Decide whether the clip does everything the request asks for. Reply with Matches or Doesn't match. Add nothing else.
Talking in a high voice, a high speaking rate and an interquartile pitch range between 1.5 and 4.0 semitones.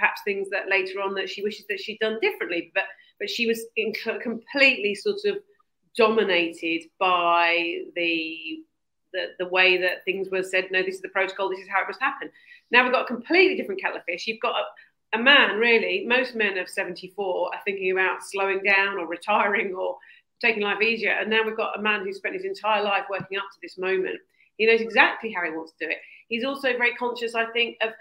Doesn't match